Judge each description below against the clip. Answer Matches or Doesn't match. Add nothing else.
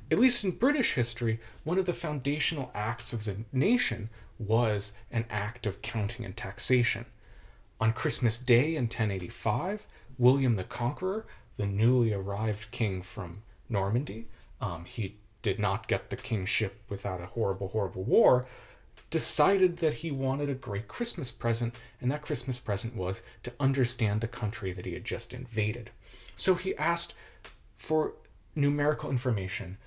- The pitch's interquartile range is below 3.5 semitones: Doesn't match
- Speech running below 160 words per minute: Matches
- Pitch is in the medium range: Doesn't match